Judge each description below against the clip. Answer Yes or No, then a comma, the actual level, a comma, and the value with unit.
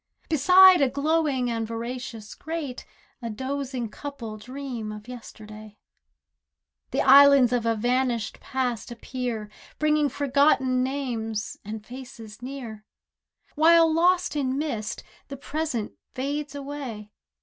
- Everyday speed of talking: No, slow, 115 wpm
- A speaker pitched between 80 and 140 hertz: No, very high, 255 Hz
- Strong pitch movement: No, average, 3.9 semitones